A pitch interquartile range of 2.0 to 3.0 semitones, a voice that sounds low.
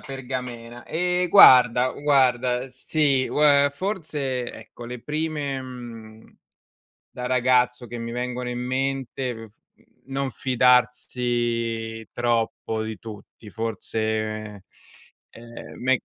Yes: narrow, 2.4 semitones; low, 125 Hz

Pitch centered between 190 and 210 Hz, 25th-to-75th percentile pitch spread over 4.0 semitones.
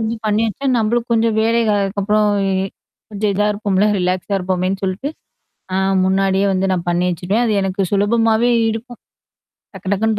No: high, 205 Hz; average, 2.7 semitones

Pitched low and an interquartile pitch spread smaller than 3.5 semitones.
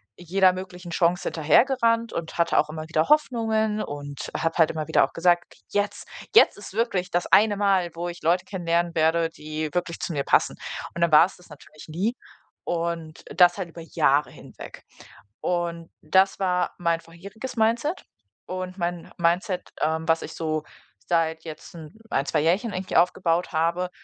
No: medium, 175 Hz; average, 2.7 semitones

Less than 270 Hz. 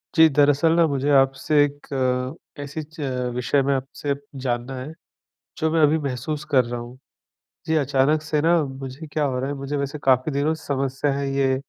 Yes: medium, 140 Hz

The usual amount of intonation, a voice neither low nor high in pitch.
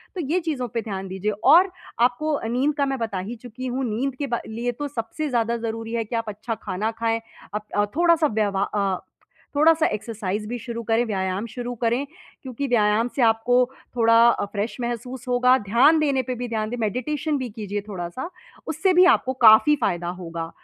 No: average, 3.8 semitones; high, 235 Hz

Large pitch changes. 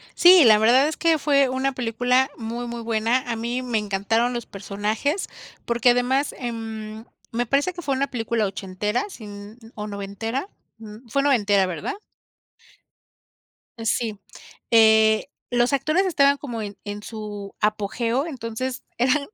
No: average, 3.6 semitones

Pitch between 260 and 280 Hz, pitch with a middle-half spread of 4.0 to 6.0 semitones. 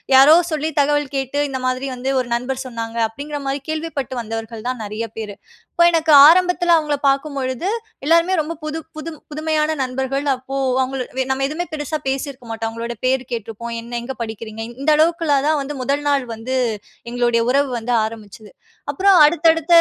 Yes: very high, 270 Hz; average, 4.4 semitones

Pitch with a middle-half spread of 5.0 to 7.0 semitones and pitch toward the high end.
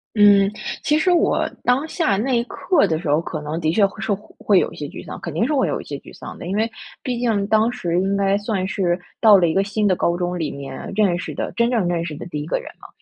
No: average, 4.5 semitones; high, 195 Hz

